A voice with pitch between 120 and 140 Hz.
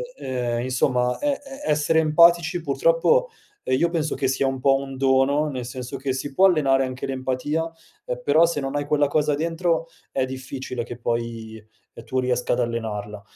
Yes: low, 135 Hz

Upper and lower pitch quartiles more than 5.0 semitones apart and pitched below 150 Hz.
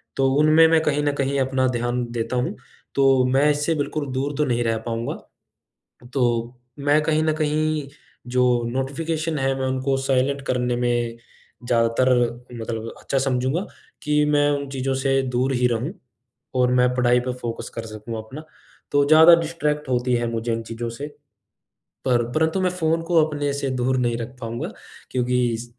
No: average, 3.3 semitones; low, 135 Hz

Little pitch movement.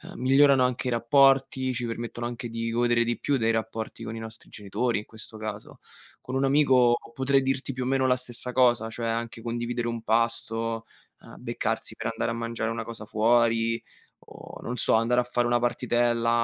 Yes: narrow, 1.7 semitones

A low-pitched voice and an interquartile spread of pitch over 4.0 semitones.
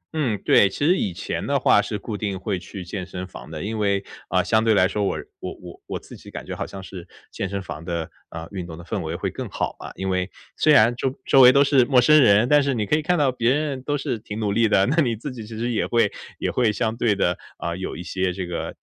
Yes: low, 105 Hz; average, 5.0 semitones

